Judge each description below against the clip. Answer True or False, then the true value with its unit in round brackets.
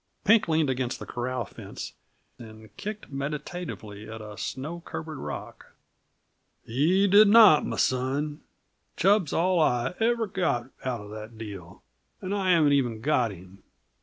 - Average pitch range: False (7.7 semitones)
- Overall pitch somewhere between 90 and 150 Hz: True (140 Hz)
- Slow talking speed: False (145 wpm)